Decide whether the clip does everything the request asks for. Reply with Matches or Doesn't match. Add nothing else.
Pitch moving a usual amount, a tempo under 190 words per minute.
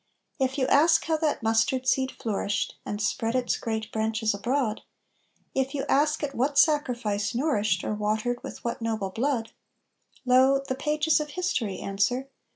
Matches